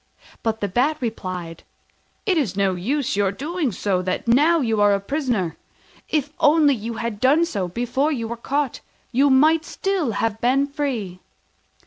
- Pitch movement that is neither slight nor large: No, wide, 6.2 semitones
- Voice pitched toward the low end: No, high, 245 Hz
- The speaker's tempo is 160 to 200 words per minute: Yes, average, 165 wpm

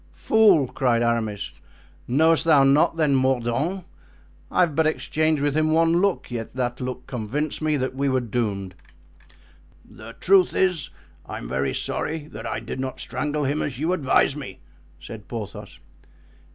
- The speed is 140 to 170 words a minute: Yes, average, 155 wpm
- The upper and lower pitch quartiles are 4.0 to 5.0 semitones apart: Yes, average, 4.7 semitones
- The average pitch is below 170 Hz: Yes, low, 135 Hz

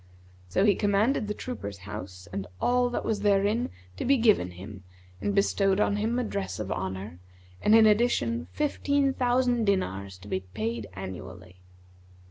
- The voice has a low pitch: No, high, 195 Hz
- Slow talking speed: No, average, 160 wpm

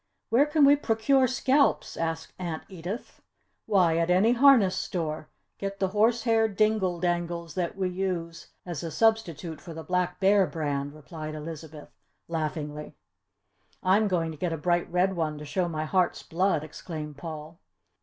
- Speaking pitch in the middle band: Yes, medium, 175 Hz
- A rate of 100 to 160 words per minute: Yes, average, 155 wpm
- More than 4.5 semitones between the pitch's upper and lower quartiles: No, average, 3.8 semitones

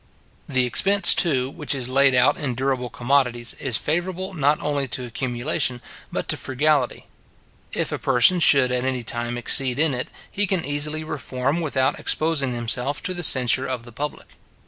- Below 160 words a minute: No, average, 170 wpm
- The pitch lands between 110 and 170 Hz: Yes, low, 135 Hz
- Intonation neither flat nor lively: Yes, average, 3.4 semitones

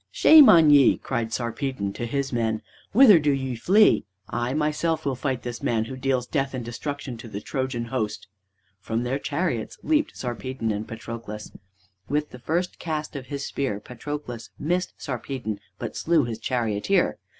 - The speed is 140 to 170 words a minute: Yes, average, 165 wpm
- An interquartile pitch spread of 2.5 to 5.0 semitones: Yes, average, 4.2 semitones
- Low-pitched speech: Yes, low, 130 Hz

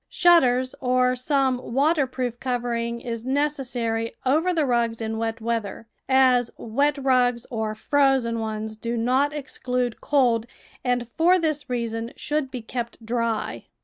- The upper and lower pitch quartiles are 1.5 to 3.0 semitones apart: Yes, average, 2.7 semitones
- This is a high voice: Yes, high, 245 Hz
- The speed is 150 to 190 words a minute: No, average, 140 wpm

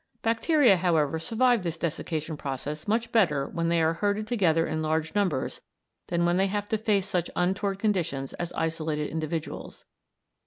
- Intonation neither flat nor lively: Yes, average, 4.5 semitones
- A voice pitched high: No, medium, 170 Hz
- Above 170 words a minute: No, average, 160 wpm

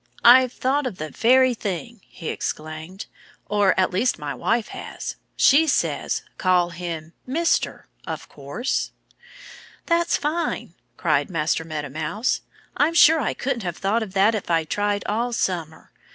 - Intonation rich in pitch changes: Yes, wide, 7.4 semitones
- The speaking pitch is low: No, high, 205 Hz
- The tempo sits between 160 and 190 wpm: No, average, 150 wpm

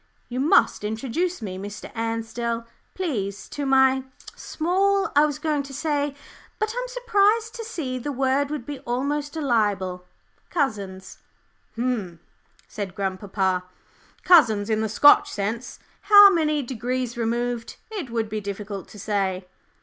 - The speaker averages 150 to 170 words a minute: No, average, 140 wpm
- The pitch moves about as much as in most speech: No, wide, 6.3 semitones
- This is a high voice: Yes, very high, 250 Hz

